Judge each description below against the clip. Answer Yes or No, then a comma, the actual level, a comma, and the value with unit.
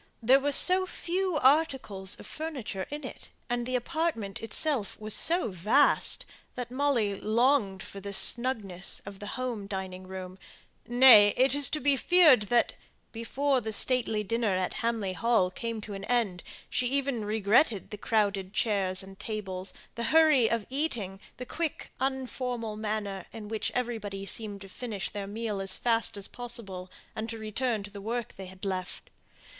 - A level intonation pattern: No, average, 4.3 semitones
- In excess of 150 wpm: Yes, average, 165 wpm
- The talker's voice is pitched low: No, high, 225 Hz